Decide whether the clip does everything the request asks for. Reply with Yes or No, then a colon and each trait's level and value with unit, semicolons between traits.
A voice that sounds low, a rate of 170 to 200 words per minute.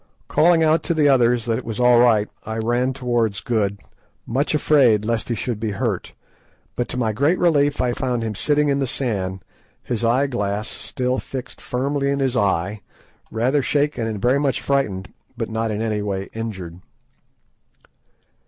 Yes: low, 120 Hz; average, 175 wpm